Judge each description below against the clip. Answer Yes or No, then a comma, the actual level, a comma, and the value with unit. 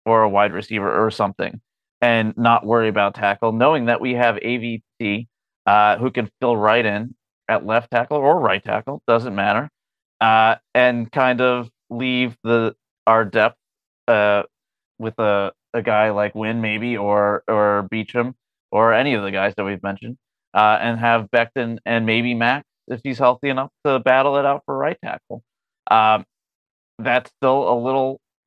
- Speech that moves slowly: No, average, 170 wpm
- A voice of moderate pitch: No, low, 115 Hz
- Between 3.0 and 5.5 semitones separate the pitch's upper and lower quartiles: No, narrow, 2.4 semitones